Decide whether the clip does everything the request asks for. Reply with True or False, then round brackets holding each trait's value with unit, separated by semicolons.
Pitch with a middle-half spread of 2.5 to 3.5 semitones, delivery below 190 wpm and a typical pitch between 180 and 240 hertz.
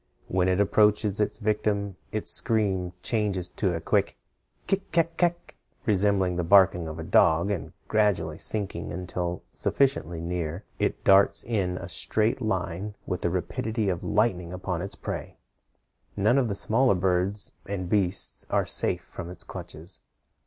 False (3.1 semitones; 150 wpm; 95 Hz)